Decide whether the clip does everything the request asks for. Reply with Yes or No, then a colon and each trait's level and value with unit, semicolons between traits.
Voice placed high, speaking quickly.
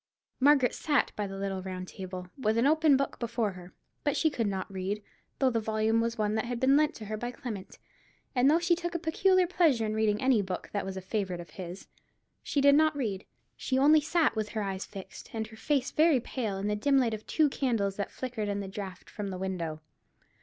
Yes: high, 220 Hz; fast, 230 wpm